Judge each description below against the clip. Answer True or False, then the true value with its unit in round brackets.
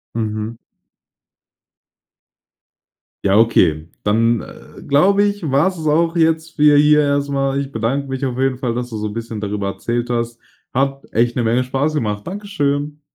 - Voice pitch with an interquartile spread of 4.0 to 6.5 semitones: True (4.4 semitones)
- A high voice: False (135 Hz)